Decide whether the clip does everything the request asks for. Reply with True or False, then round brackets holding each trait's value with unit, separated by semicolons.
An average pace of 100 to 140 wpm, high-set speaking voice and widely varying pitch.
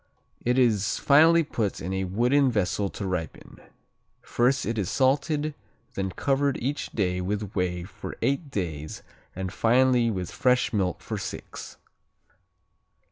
False (135 wpm; 115 Hz; 6.3 semitones)